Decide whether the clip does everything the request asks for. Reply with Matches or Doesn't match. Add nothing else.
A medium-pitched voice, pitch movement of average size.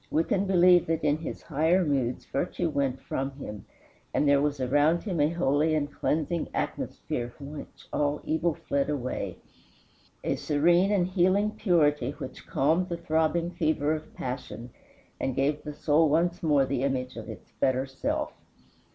Matches